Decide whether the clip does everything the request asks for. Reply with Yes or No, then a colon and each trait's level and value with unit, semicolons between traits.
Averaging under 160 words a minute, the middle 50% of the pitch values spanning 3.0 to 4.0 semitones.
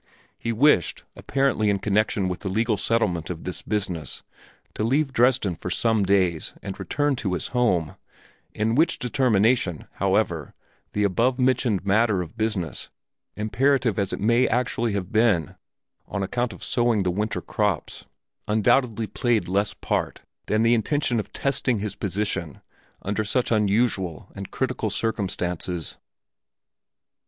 Yes: average, 140 wpm; average, 3.7 semitones